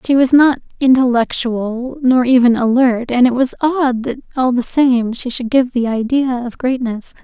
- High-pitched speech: Yes, very high, 250 Hz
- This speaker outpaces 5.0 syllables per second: No, 4.4 syllables/s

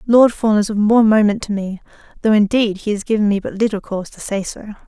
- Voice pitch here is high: Yes, high, 210 Hz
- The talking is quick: Yes, fast, 235 wpm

